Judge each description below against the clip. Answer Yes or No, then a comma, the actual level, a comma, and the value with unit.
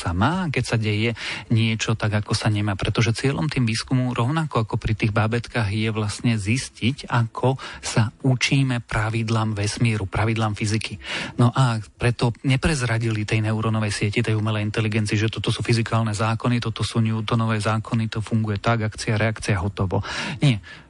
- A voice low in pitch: Yes, low, 115 Hz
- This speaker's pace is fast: No, average, 155 wpm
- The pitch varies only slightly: Yes, narrow, 1.8 semitones